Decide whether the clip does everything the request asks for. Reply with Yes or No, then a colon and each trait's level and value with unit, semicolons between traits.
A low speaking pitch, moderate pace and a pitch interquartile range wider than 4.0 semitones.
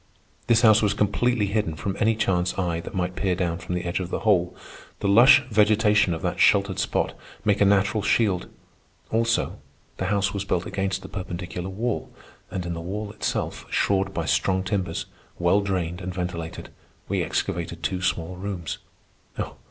No: very low, 95 Hz; average, 175 wpm; average, 2.7 semitones